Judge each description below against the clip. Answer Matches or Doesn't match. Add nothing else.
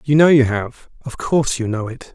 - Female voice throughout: Doesn't match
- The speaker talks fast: Matches